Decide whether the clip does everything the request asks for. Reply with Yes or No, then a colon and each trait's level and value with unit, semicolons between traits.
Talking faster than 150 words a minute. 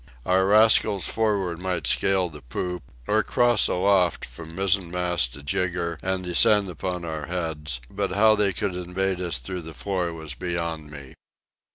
Yes: average, 160 wpm